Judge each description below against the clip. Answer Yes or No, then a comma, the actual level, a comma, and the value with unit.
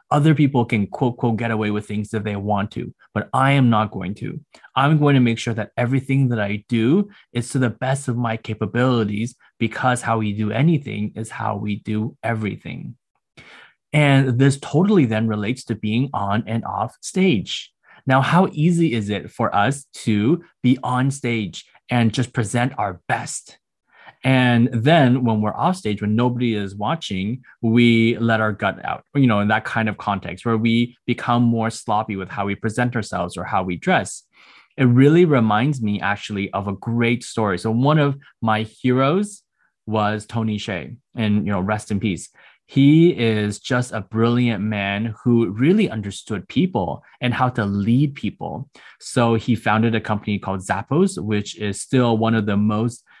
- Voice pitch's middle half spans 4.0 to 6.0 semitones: No, average, 3.4 semitones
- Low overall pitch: Yes, low, 115 Hz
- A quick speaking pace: No, average, 180 wpm